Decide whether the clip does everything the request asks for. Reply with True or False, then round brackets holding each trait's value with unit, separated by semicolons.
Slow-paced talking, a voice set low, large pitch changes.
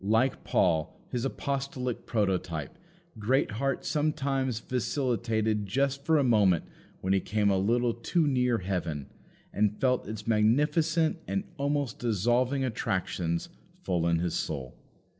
True (125 wpm; 115 Hz; 5.8 semitones)